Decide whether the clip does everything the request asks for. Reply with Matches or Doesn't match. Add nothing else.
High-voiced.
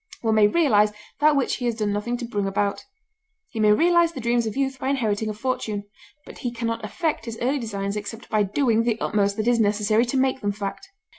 Matches